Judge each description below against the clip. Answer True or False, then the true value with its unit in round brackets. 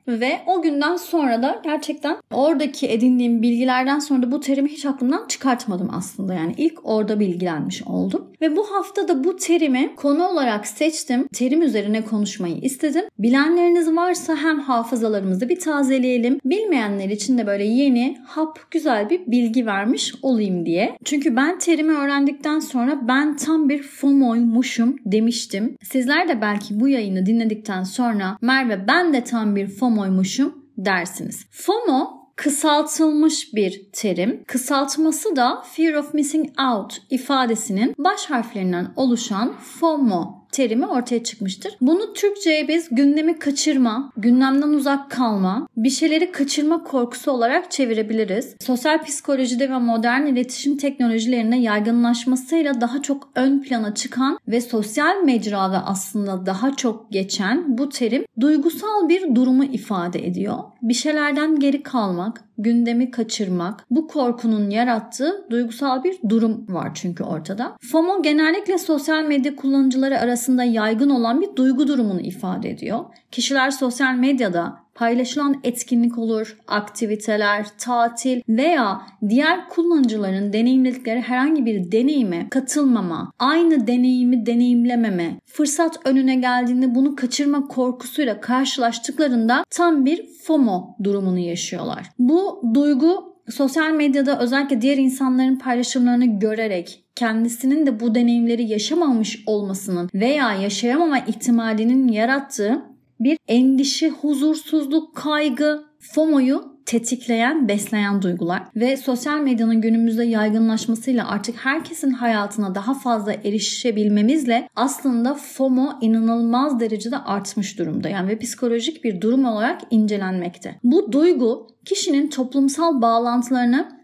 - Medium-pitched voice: False (250 Hz)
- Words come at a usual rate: True (120 wpm)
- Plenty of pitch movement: False (4.4 semitones)